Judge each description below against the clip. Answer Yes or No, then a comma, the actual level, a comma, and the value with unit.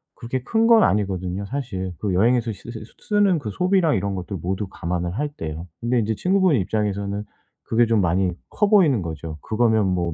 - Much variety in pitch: Yes, wide, 6.1 semitones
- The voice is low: Yes, low, 105 Hz